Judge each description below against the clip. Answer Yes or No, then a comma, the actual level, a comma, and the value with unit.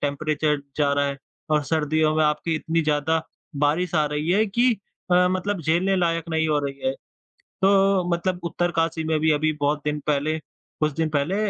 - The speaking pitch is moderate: Yes, medium, 160 Hz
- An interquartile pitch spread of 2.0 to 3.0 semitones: Yes, average, 2.7 semitones